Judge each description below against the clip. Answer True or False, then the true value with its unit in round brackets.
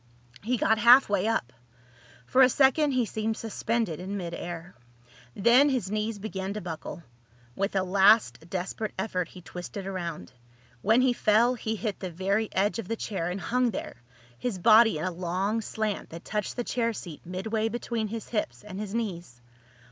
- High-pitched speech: True (210 Hz)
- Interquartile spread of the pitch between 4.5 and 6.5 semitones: False (3.7 semitones)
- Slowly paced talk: False (180 wpm)